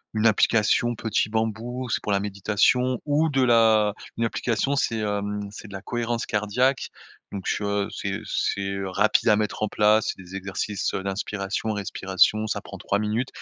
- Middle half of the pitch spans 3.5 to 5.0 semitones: No, narrow, 2.4 semitones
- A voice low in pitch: Yes, low, 105 Hz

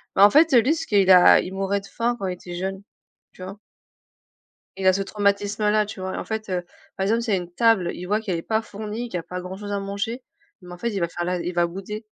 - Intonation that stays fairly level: No, average, 3.0 semitones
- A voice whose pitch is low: No, high, 200 Hz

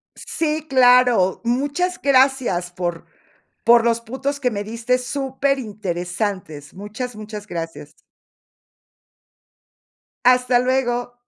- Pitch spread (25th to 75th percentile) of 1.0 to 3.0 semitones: No, average, 4.3 semitones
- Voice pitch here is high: Yes, high, 240 Hz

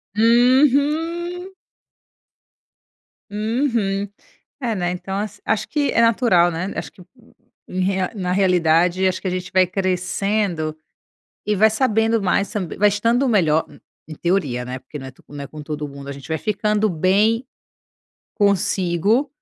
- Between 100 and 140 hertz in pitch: No, high, 195 Hz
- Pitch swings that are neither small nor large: Yes, average, 4.2 semitones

